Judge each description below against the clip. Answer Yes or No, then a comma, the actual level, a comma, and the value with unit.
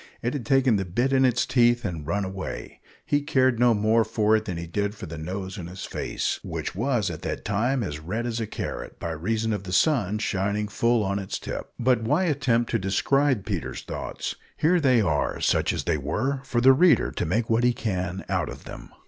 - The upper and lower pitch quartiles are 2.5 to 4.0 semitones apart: No, average, 4.5 semitones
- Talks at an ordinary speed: No, fast, 225 wpm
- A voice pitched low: Yes, low, 110 Hz